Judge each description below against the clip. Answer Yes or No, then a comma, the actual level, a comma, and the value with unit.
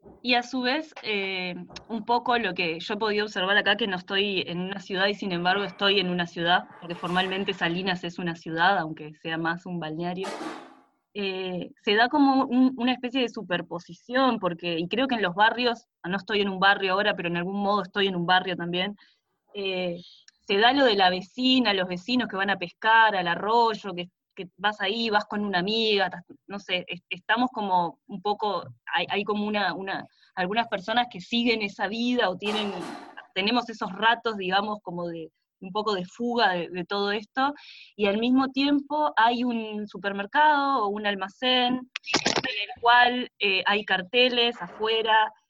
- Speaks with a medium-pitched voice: No, high, 200 Hz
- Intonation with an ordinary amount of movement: Yes, average, 4.2 semitones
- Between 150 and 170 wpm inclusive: No, average, 185 wpm